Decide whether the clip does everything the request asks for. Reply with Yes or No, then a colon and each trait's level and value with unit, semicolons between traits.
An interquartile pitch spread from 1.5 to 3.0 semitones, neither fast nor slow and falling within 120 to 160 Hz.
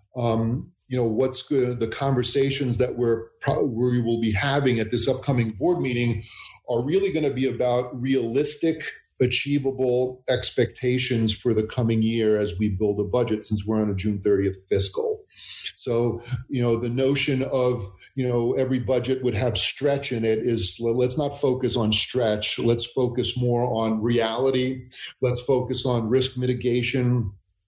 Yes: narrow, 2.5 semitones; average, 165 wpm; low, 125 Hz